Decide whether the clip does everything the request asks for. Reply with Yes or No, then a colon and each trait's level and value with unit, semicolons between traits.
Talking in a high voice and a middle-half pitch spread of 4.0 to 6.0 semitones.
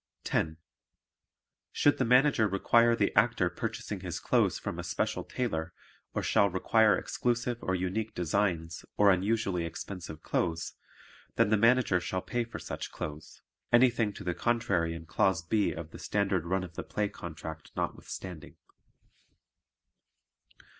No: very low, 95 Hz; average, 5.1 semitones